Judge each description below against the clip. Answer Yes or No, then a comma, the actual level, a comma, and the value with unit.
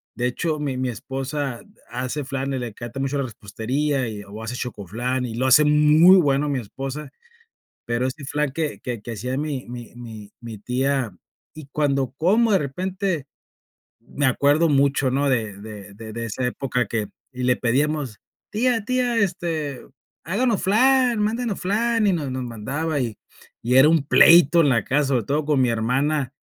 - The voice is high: No, low, 135 Hz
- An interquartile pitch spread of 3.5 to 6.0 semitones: Yes, average, 4.1 semitones